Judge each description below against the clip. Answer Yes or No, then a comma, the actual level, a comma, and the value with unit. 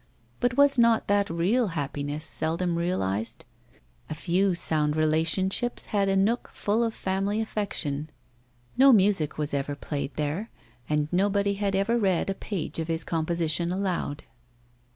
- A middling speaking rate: Yes, average, 145 wpm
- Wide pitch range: No, average, 4.7 semitones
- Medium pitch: Yes, medium, 180 Hz